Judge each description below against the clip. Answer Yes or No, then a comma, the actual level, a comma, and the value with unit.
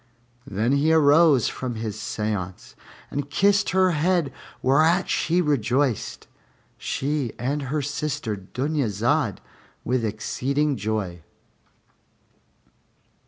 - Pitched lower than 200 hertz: Yes, medium, 140 Hz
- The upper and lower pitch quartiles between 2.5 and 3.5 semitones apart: No, wide, 5.5 semitones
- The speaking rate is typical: No, slow, 95 wpm